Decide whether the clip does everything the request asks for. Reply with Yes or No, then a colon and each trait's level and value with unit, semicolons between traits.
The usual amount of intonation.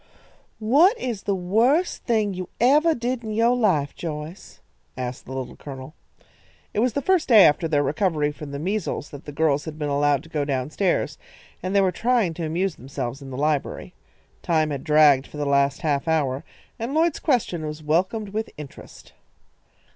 No: wide, 7.1 semitones